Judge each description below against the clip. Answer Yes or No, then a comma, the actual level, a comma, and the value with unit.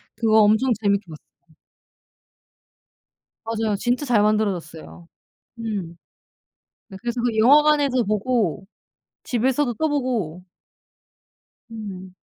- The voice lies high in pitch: Yes, high, 220 Hz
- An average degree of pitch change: Yes, average, 3.8 semitones